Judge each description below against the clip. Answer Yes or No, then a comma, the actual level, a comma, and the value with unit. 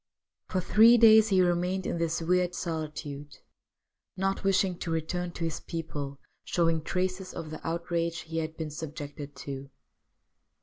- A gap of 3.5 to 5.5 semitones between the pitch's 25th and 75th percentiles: No, average, 2.8 semitones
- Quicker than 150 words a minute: No, average, 145 wpm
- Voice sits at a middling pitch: Yes, medium, 165 Hz